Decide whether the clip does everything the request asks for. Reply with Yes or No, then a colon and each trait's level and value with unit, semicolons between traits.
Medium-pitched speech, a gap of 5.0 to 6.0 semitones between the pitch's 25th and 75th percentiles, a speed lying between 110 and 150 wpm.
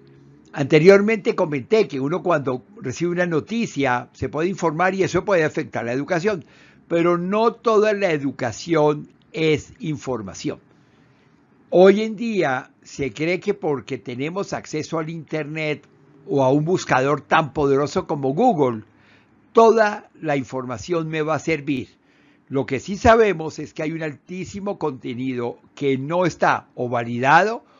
Yes: medium, 155 Hz; wide, 5.5 semitones; average, 140 wpm